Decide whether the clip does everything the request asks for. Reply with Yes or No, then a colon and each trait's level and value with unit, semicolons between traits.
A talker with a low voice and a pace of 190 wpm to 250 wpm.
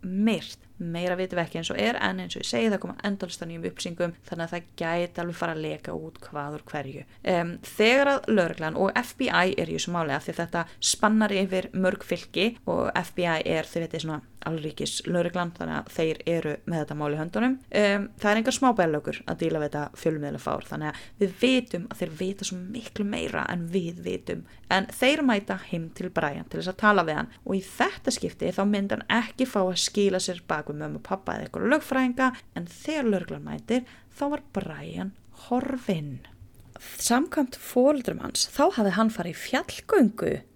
No: medium, 180 Hz; average, 195 wpm